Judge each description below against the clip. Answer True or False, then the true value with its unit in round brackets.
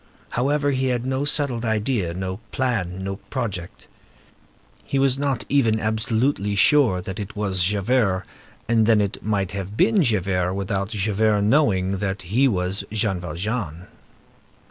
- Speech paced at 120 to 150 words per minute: True (145 wpm)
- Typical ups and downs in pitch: True (4.7 semitones)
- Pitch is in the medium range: False (105 Hz)